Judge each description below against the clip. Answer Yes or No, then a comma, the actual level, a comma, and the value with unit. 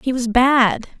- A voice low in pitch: No, high, 245 Hz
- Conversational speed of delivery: Yes, average, 180 wpm